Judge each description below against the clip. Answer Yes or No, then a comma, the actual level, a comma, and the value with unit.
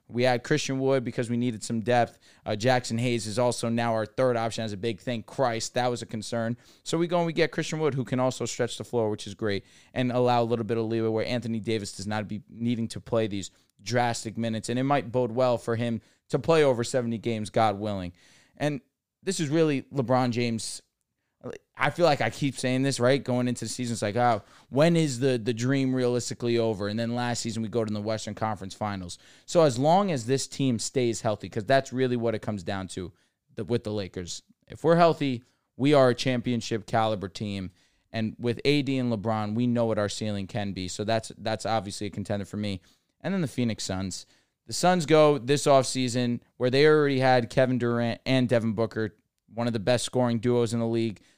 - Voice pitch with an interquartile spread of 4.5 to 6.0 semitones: No, average, 2.7 semitones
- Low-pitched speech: Yes, low, 120 Hz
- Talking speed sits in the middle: No, fast, 225 wpm